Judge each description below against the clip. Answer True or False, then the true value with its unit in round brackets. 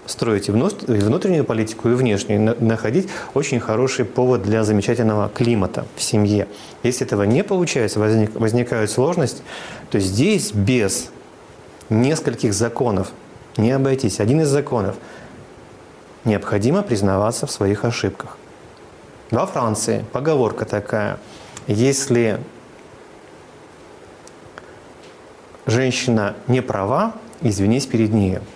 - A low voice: True (115 Hz)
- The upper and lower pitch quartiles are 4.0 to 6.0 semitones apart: False (3.3 semitones)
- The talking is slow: True (100 wpm)